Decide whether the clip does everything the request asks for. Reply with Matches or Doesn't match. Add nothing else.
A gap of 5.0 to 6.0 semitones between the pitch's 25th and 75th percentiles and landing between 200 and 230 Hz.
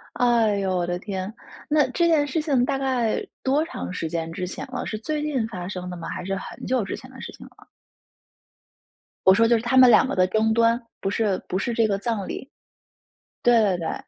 Matches